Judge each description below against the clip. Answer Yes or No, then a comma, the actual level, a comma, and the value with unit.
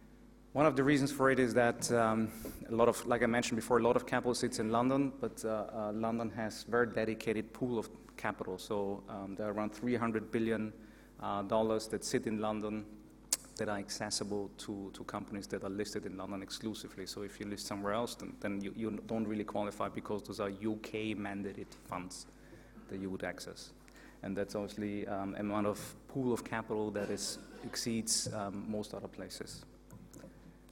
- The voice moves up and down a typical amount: No, narrow, 2.3 semitones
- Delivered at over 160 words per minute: Yes, average, 190 wpm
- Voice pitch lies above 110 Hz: No, low, 105 Hz